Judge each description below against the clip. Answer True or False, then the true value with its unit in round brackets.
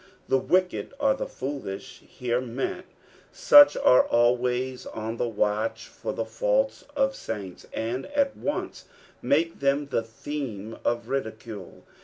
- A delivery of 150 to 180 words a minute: False (135 wpm)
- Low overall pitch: True (125 Hz)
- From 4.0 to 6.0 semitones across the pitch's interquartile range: True (4.5 semitones)